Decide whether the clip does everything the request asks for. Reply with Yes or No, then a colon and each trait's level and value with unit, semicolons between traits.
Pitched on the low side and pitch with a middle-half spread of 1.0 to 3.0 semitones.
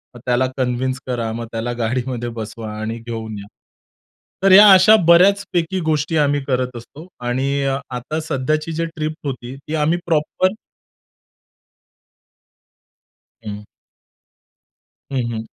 No: low, 130 Hz; average, 4.7 semitones